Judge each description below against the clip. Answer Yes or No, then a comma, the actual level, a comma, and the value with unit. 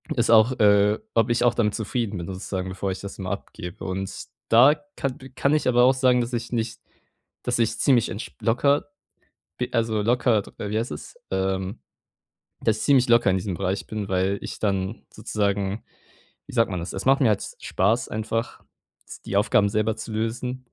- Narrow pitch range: No, average, 3.4 semitones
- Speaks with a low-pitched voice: Yes, low, 110 Hz